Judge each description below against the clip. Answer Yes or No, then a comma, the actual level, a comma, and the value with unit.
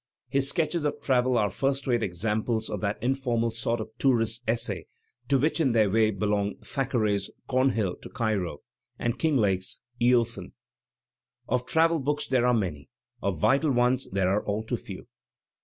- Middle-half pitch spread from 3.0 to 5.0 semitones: Yes, average, 4.1 semitones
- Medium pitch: No, low, 120 Hz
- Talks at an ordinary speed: Yes, average, 160 wpm